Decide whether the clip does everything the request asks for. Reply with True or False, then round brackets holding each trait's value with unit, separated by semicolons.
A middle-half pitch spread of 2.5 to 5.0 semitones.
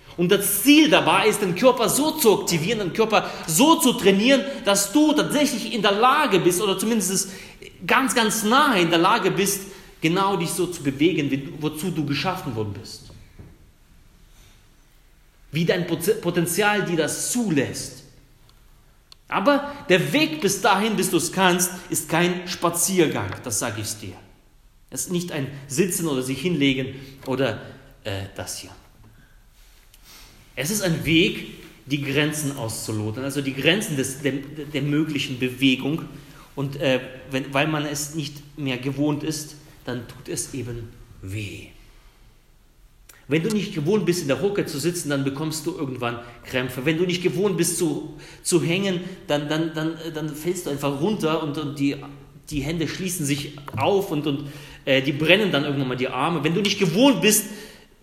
False (5.6 semitones)